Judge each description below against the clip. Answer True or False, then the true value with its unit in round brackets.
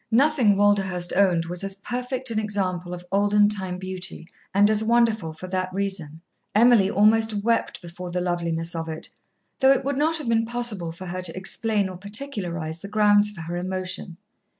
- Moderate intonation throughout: True (3.6 semitones)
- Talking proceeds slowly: False (180 wpm)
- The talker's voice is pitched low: False (195 Hz)